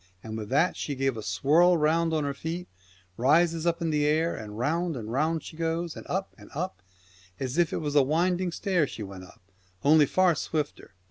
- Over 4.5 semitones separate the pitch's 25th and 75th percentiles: No, average, 3.9 semitones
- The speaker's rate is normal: No, fast, 215 wpm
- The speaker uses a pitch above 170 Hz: No, medium, 155 Hz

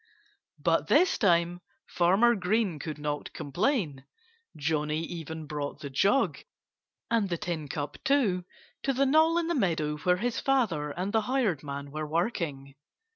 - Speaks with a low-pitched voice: No, medium, 175 Hz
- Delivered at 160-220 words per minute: No, average, 150 wpm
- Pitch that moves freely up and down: Yes, wide, 7.3 semitones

